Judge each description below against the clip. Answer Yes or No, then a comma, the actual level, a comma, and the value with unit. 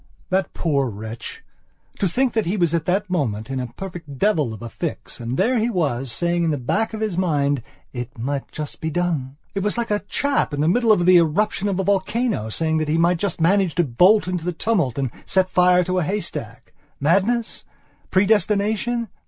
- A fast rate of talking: Yes, fast, 210 wpm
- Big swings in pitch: Yes, wide, 6.0 semitones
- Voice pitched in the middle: Yes, medium, 175 Hz